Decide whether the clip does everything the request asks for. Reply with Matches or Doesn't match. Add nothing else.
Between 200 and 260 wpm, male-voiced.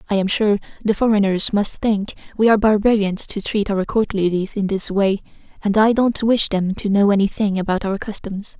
Doesn't match